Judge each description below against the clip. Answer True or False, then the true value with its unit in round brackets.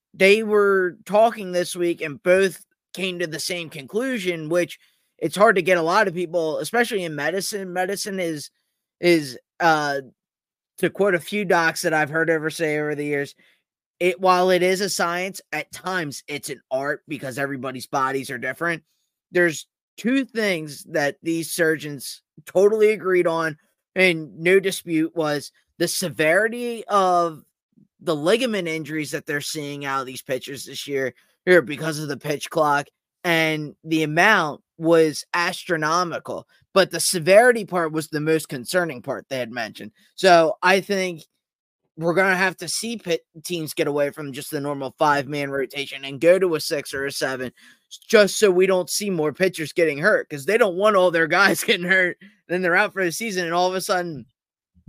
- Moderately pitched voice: True (170 Hz)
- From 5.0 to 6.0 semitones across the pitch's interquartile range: False (3.8 semitones)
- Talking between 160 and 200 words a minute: True (180 wpm)